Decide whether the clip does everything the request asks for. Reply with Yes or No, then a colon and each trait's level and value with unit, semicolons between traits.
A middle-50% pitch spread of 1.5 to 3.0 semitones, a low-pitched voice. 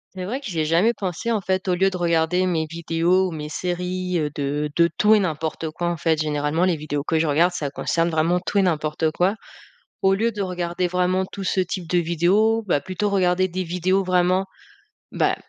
No: narrow, 2.6 semitones; medium, 180 Hz